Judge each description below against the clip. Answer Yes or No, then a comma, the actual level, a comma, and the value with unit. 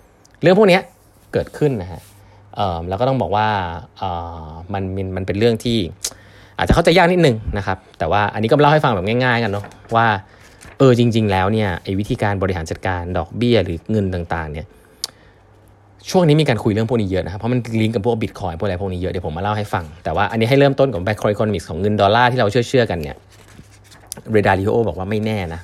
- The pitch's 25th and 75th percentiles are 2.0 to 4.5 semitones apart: Yes, average, 3.3 semitones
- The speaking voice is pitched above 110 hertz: No, low, 105 Hz